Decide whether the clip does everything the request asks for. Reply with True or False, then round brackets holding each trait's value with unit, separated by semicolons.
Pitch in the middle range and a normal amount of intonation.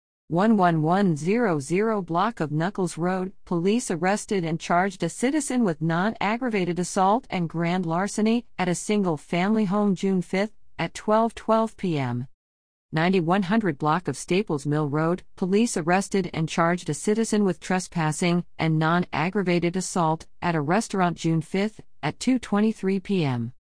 True (180 Hz; 3.9 semitones)